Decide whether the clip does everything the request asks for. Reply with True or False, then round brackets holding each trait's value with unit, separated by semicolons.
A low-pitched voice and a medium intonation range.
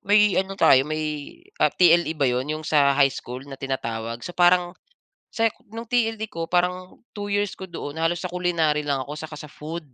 False (160 Hz; 4.2 semitones)